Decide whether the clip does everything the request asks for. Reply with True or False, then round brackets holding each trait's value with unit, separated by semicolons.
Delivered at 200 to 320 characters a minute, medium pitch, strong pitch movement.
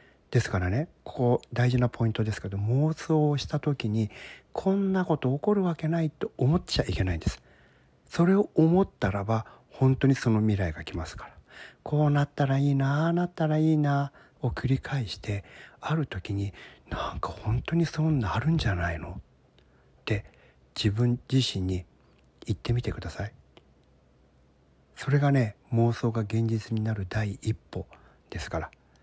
False (315 characters per minute; 115 Hz; 6.9 semitones)